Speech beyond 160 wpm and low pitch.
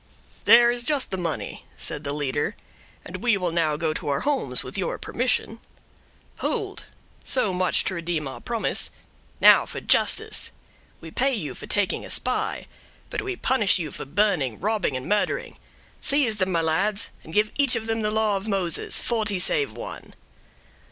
No: average, 170 wpm; high, 200 Hz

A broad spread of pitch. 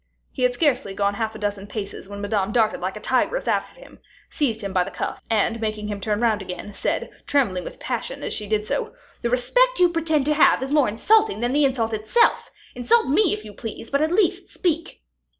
Yes: wide, 6.5 semitones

